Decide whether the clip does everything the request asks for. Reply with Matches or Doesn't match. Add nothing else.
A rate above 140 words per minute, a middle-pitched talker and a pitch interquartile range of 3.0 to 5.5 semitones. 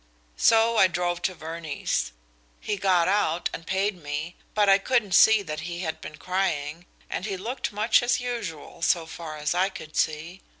Matches